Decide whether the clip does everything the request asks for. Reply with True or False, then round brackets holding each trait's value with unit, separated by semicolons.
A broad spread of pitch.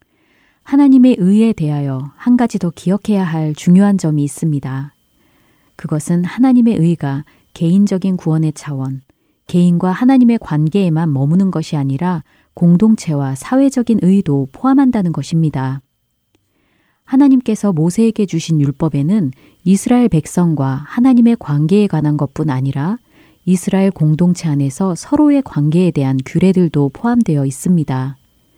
True (5.8 semitones)